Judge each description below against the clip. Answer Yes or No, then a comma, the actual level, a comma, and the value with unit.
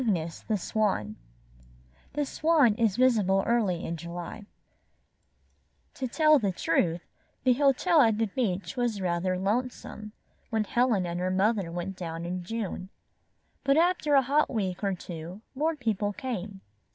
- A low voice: No, high, 210 Hz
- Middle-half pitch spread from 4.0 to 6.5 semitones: Yes, wide, 5.6 semitones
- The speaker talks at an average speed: Yes, average, 145 wpm